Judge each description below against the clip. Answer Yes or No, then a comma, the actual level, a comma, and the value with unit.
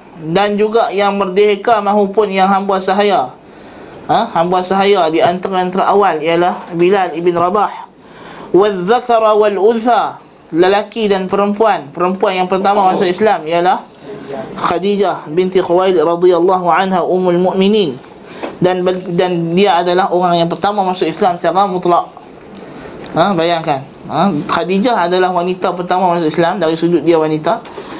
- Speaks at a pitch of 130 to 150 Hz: No, medium, 185 Hz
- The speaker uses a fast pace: No, average, 135 wpm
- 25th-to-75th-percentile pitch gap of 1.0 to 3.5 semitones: Yes, narrow, 2.5 semitones